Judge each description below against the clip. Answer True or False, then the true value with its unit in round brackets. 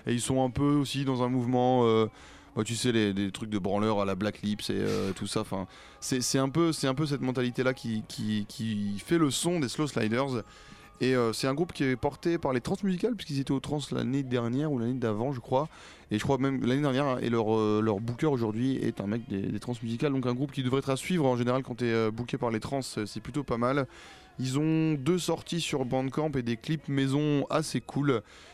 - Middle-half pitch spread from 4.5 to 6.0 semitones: False (4.0 semitones)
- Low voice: True (130 Hz)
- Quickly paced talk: True (250 wpm)